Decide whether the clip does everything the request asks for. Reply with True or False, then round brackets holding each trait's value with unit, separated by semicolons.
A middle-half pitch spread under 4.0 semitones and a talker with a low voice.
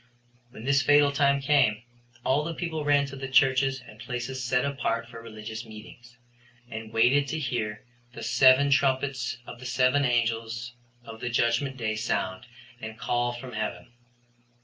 True (2.9 semitones; 125 Hz)